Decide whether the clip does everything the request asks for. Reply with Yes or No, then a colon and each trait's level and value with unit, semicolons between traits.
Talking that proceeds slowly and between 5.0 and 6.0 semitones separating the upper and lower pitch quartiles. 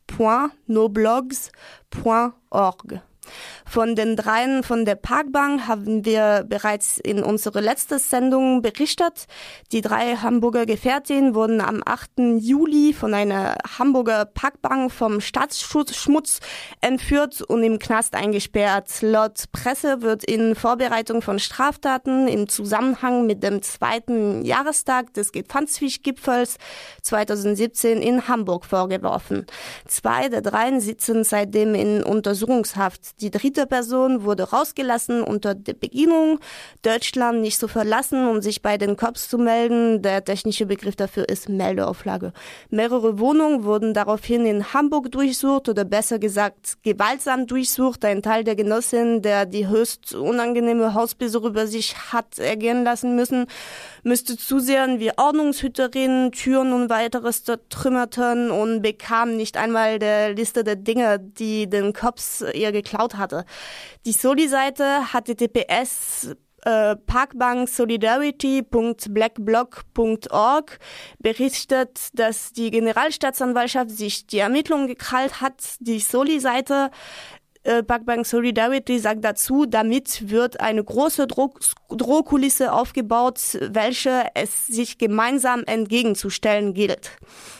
No: slow, 120 wpm; average, 3.1 semitones